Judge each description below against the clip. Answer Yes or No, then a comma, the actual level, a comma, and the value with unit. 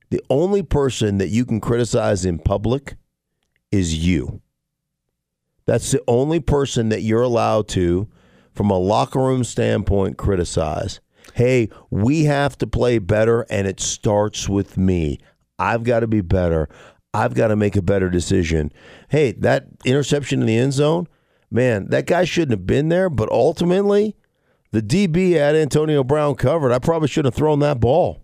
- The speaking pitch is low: Yes, low, 120 Hz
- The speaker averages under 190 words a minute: Yes, average, 165 wpm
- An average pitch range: No, wide, 6.2 semitones